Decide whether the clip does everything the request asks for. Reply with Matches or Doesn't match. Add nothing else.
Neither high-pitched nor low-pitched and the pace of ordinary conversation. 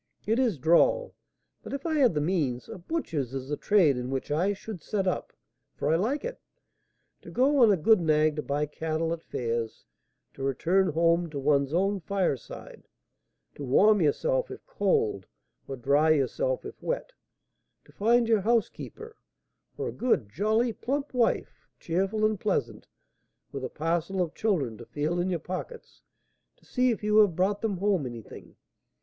Matches